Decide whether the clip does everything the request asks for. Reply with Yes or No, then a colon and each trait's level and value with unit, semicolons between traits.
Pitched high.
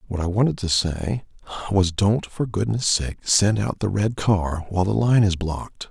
No: low, 100 Hz